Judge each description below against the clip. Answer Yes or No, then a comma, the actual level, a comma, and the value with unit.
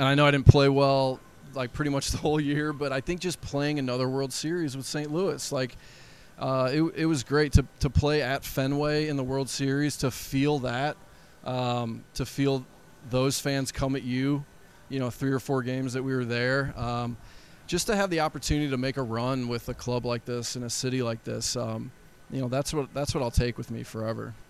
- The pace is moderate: No, fast, 225 wpm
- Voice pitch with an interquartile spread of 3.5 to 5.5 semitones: No, average, 2.7 semitones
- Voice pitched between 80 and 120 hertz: No, low, 135 Hz